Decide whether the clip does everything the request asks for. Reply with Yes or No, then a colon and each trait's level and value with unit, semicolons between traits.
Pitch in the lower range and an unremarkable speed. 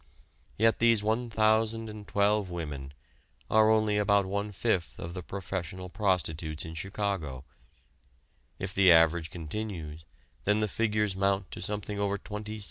No: low, 100 Hz; slow, 130 wpm